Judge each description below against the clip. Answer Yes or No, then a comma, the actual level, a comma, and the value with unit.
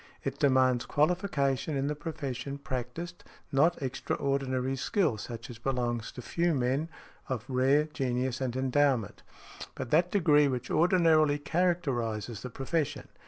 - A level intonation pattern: No, average, 3.5 semitones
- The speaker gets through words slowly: Yes, slow, 130 wpm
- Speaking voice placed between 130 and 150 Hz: Yes, low, 135 Hz